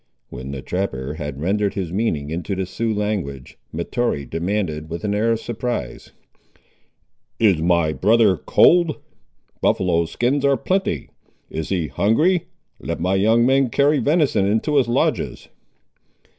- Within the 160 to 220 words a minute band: No, average, 140 wpm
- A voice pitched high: No, low, 100 Hz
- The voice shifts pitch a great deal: Yes, wide, 6.4 semitones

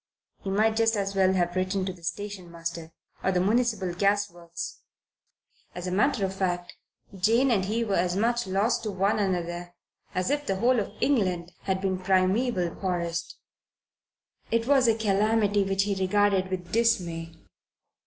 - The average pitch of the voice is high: Yes, high, 195 Hz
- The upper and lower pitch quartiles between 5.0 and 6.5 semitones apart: No, average, 3.1 semitones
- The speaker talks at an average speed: Yes, average, 165 wpm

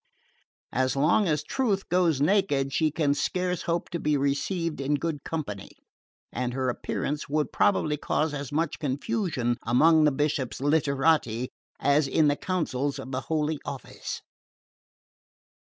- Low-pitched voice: No, medium, 150 Hz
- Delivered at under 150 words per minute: Yes, average, 140 wpm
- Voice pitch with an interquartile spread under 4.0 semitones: Yes, average, 3.1 semitones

